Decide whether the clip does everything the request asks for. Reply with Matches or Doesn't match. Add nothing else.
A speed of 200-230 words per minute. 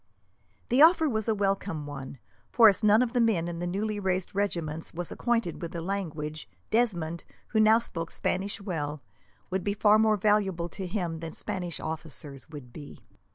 Doesn't match